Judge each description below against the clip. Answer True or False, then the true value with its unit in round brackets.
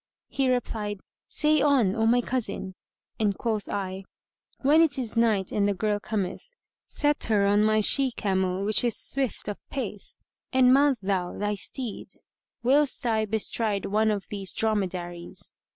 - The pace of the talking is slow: False (155 wpm)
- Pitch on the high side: True (215 Hz)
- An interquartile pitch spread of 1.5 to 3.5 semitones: False (4.1 semitones)